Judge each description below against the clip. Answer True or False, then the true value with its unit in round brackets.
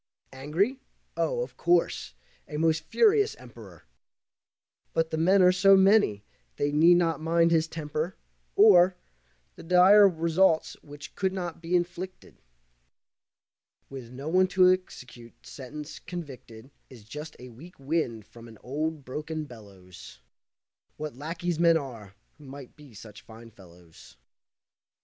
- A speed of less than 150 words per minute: True (135 wpm)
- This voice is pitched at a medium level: True (160 Hz)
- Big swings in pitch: True (5.7 semitones)